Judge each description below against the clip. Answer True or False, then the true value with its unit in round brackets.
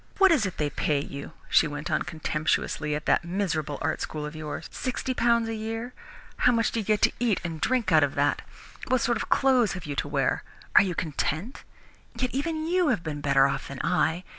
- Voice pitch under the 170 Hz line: False (185 Hz)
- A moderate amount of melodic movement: False (8.1 semitones)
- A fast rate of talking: True (220 wpm)